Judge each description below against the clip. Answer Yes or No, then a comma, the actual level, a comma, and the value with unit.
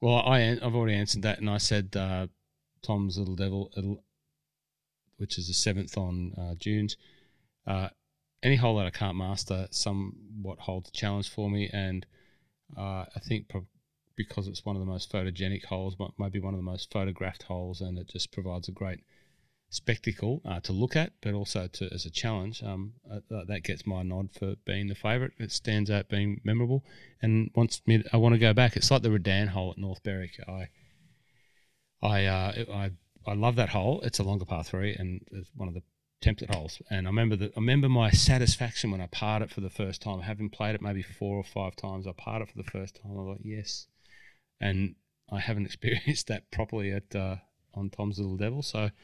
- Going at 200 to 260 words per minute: Yes, fast, 205 wpm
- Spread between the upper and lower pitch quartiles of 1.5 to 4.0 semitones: Yes, average, 2.7 semitones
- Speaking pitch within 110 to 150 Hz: No, low, 100 Hz